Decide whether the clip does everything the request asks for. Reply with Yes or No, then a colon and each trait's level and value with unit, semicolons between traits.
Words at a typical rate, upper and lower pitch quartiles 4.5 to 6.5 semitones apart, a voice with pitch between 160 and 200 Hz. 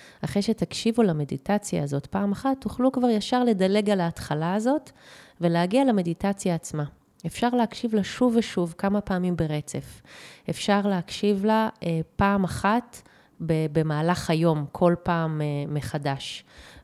Yes: average, 130 wpm; average, 4.9 semitones; high, 190 Hz